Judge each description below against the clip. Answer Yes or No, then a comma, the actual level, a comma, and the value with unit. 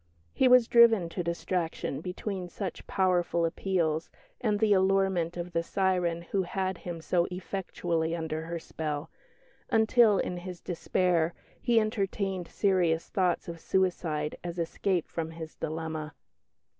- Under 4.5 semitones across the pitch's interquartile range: Yes, narrow, 2.6 semitones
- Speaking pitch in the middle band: Yes, medium, 175 Hz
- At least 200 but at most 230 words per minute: No, slow, 135 wpm